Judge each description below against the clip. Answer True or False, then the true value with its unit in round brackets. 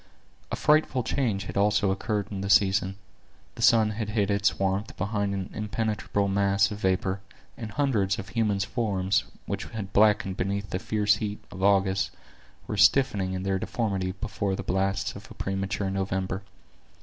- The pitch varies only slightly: True (1.7 semitones)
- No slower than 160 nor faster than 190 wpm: True (165 wpm)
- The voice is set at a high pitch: False (100 Hz)